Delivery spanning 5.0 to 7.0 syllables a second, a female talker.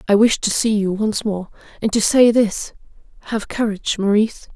Yes: 5.2 syllables/s; female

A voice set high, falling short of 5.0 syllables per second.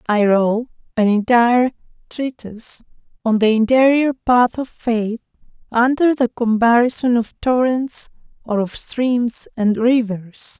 Yes: high, 235 Hz; 4.0 syllables/s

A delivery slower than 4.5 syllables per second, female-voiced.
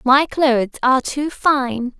Yes: 3.8 syllables/s; female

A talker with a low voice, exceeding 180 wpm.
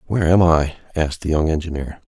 Yes: very low, 80 Hz; average, 200 wpm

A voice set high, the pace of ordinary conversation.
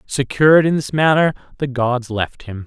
No: low, 135 Hz; average, 180 wpm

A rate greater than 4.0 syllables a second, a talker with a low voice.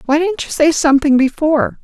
No: 5.9 syllables/s; very high, 300 Hz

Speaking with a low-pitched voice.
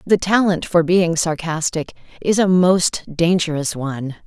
No: medium, 170 Hz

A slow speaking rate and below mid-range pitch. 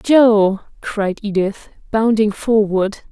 No: slow, 95 wpm; high, 210 Hz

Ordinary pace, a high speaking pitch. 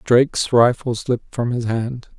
No: average, 165 wpm; low, 120 Hz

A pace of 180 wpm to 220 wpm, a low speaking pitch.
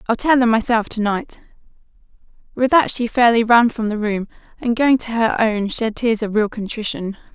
No: average, 195 wpm; high, 225 Hz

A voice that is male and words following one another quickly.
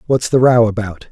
Yes: male; fast, 215 wpm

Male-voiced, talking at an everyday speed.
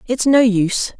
No: female; average, 180 wpm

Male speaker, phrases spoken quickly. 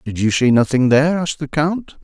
Yes: male; fast, 235 wpm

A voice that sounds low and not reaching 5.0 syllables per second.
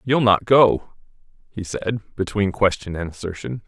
Yes: low, 105 Hz; 4.5 syllables/s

